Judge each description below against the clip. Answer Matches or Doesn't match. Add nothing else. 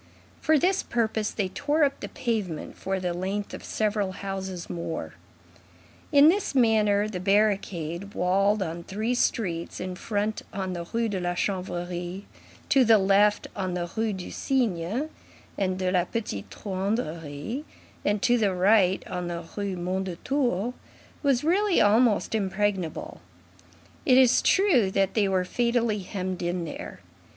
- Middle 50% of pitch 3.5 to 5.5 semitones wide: Matches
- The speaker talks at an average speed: Matches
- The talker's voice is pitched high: Matches